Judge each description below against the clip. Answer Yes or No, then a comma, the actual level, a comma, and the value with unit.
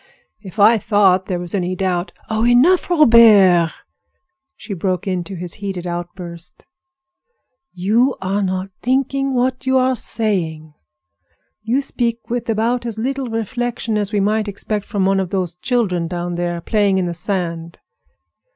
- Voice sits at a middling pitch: No, high, 200 Hz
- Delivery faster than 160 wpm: No, average, 150 wpm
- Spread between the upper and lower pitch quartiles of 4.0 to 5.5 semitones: Yes, average, 4.6 semitones